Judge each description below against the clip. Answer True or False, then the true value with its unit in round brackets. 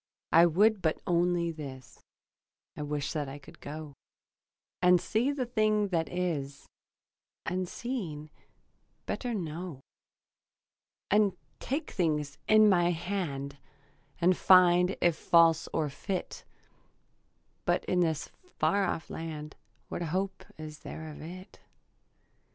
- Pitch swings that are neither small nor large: True (3.8 semitones)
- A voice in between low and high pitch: True (170 Hz)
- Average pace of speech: False (120 wpm)